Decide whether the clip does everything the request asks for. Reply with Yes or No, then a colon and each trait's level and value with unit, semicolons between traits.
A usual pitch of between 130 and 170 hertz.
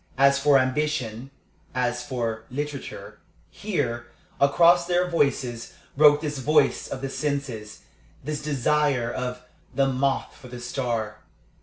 Yes: low, 135 Hz